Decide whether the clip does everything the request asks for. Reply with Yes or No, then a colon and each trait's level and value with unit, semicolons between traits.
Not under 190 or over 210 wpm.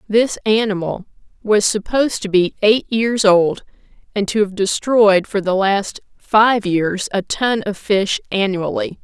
No: average, 155 wpm